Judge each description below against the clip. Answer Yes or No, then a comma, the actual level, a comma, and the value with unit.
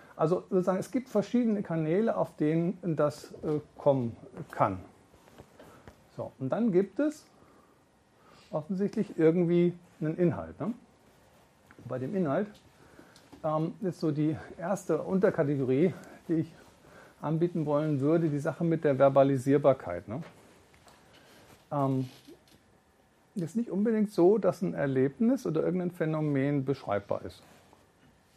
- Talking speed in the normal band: No, slow, 115 wpm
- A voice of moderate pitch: Yes, medium, 160 Hz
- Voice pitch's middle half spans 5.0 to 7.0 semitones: No, average, 4.6 semitones